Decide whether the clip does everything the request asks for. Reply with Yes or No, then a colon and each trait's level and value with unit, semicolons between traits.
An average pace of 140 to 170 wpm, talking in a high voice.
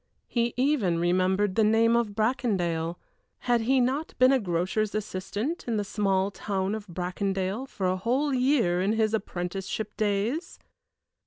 Yes: average, 150 wpm; high, 210 Hz